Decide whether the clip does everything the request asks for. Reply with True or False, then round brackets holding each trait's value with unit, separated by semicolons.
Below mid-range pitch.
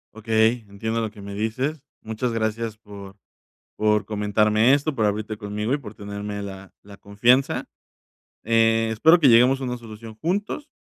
True (110 Hz)